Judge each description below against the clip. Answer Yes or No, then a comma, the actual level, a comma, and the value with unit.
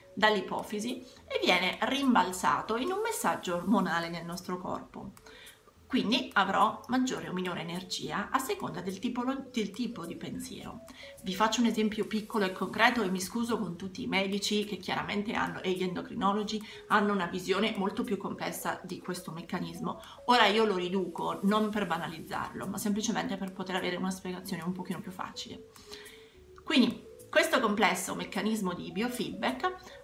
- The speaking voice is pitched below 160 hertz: No, high, 205 Hz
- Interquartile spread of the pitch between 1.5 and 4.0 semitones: Yes, average, 3.6 semitones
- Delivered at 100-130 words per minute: No, average, 155 wpm